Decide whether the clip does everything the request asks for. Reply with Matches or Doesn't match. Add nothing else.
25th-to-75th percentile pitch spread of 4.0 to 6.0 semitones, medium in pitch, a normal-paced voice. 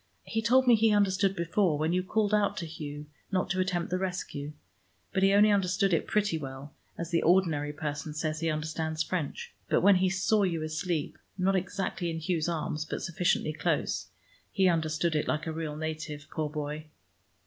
Doesn't match